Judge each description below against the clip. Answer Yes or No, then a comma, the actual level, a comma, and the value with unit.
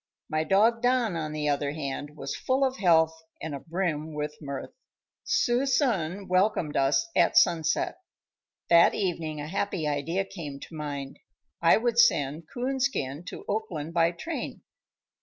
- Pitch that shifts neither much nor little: No, wide, 6.5 semitones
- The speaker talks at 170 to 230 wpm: No, average, 140 wpm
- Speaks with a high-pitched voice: No, medium, 165 Hz